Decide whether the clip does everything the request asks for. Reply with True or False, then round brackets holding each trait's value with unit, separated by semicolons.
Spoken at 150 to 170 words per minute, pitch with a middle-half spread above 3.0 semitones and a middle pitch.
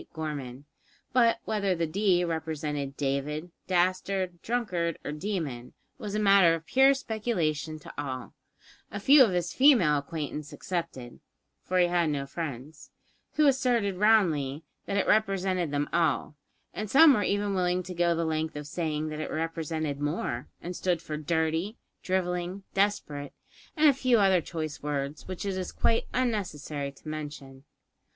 True (155 wpm; 4.8 semitones; 170 Hz)